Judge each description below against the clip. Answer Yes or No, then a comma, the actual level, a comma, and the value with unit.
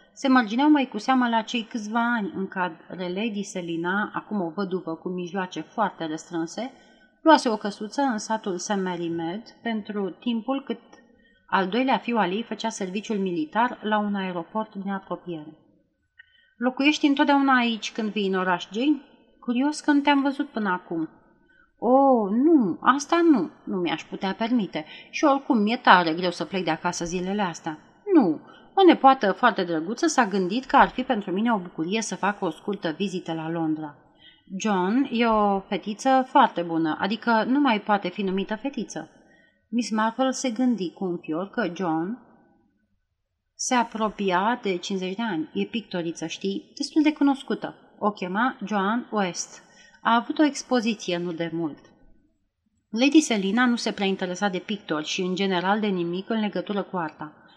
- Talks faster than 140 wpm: Yes, average, 165 wpm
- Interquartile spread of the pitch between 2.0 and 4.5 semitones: No, wide, 5.4 semitones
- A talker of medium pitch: No, high, 210 Hz